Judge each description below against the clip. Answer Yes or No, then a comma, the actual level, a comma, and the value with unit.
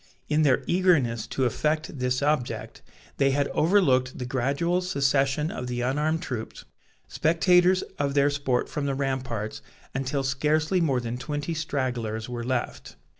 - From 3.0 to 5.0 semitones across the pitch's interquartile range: Yes, average, 3.4 semitones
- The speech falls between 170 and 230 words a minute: No, average, 145 wpm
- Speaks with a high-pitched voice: No, medium, 140 Hz